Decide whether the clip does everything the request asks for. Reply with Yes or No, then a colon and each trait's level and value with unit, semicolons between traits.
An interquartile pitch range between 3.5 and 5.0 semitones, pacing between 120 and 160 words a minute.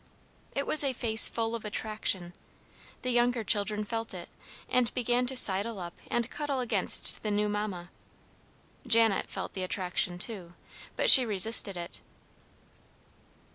Yes: average, 3.8 semitones; average, 140 wpm